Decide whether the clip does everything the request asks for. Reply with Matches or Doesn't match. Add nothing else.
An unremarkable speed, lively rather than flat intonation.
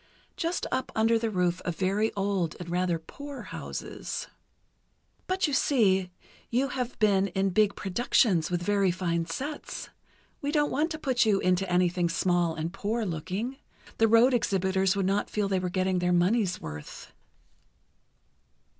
Doesn't match